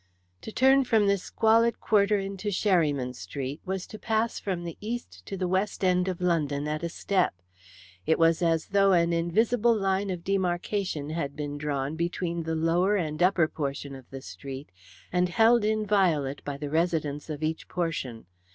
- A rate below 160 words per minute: No, average, 175 wpm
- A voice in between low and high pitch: Yes, medium, 175 Hz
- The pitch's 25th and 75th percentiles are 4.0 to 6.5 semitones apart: Yes, average, 4.8 semitones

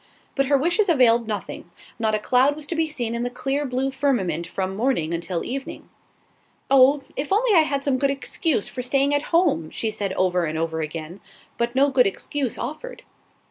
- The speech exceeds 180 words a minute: Yes, average, 195 wpm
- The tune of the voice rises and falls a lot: Yes, wide, 6.2 semitones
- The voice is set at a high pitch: Yes, very high, 255 Hz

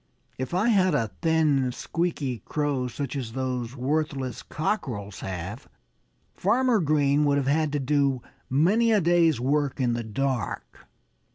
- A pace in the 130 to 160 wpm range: Yes, average, 145 wpm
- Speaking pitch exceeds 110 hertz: Yes, medium, 140 Hz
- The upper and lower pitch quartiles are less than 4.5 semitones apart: Yes, average, 4.1 semitones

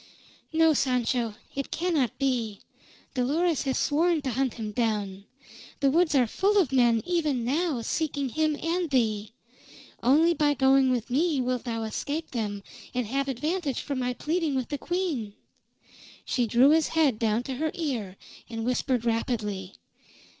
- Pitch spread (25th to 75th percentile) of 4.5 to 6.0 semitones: Yes, average, 5.0 semitones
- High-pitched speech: Yes, very high, 265 Hz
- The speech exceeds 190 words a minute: No, average, 155 wpm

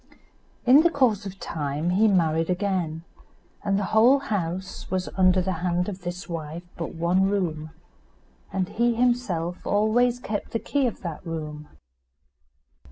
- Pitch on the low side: No, medium, 185 Hz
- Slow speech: No, average, 150 wpm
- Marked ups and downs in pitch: No, average, 4.4 semitones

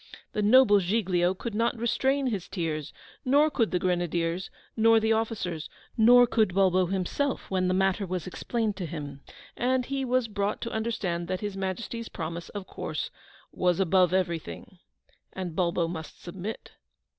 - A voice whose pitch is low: No, high, 190 Hz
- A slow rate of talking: No, average, 160 wpm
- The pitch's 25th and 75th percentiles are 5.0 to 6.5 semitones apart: No, average, 4.4 semitones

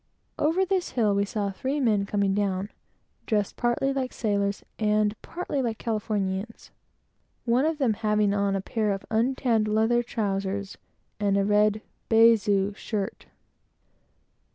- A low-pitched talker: No, high, 215 Hz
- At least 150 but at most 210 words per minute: No, slow, 135 wpm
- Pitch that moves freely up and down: No, average, 3.0 semitones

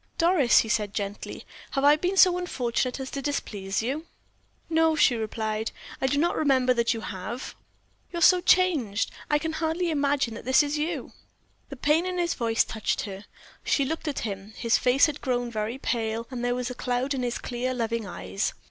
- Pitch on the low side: No, very high, 255 Hz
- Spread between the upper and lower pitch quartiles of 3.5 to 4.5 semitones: No, average, 5.0 semitones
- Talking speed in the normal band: Yes, average, 195 wpm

